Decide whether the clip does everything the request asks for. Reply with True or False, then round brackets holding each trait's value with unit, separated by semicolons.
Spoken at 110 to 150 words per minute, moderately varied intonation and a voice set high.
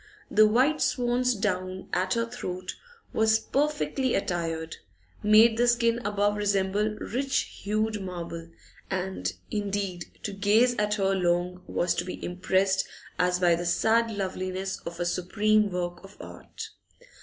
True (145 wpm; 3.3 semitones; 200 Hz)